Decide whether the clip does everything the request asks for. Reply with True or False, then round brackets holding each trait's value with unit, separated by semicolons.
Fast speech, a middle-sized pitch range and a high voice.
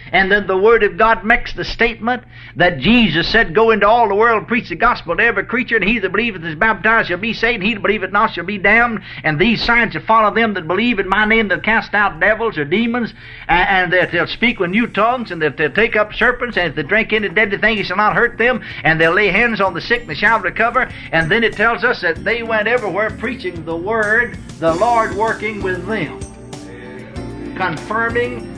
True (235 wpm; 3.9 semitones; 215 Hz)